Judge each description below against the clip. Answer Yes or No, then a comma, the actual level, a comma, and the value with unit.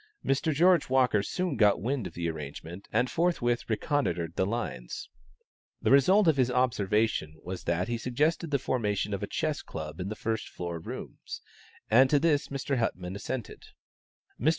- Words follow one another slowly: No, average, 170 wpm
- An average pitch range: No, wide, 6.9 semitones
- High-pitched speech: No, low, 115 Hz